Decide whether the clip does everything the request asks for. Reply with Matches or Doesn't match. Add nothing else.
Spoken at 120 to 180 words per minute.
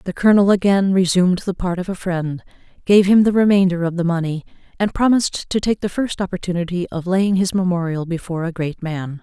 Doesn't match